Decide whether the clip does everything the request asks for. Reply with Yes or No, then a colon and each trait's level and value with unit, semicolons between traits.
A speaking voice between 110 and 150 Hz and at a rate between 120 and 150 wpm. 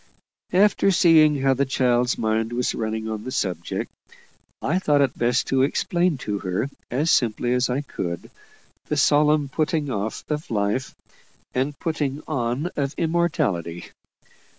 Yes: low, 135 Hz; average, 145 wpm